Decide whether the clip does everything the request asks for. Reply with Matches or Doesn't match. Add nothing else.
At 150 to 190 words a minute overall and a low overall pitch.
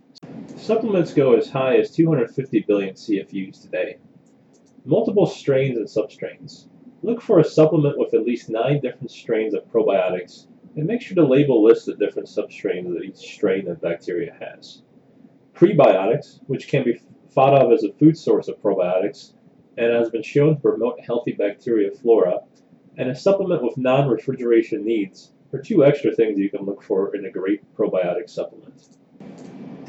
Doesn't match